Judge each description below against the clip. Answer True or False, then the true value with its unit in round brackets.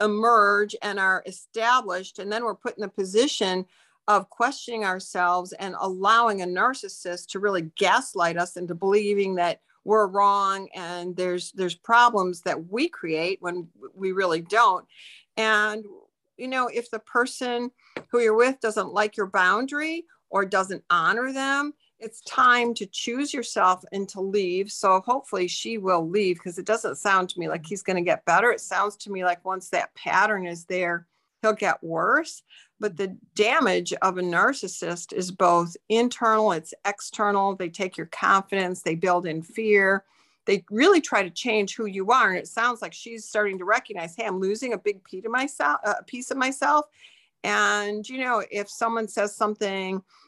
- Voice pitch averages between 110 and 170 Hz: False (200 Hz)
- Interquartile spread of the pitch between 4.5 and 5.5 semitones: False (3.6 semitones)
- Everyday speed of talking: True (170 wpm)